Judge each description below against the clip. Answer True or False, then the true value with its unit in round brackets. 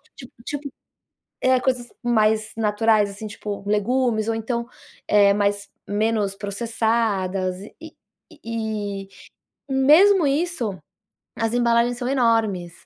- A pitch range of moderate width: True (3.1 semitones)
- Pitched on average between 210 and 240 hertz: True (225 Hz)